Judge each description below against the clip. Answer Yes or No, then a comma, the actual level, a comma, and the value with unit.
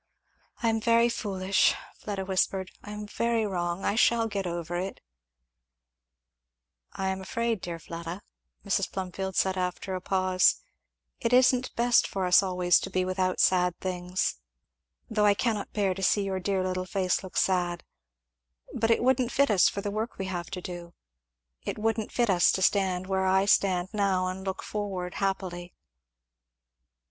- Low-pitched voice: No, high, 190 Hz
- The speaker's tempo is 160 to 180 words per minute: Yes, average, 170 wpm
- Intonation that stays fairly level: Yes, narrow, 2.3 semitones